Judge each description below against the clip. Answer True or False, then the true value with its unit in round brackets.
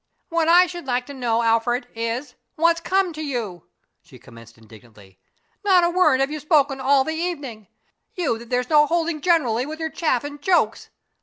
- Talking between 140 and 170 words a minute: False (185 wpm)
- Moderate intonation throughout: False (6.0 semitones)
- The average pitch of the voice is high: True (280 Hz)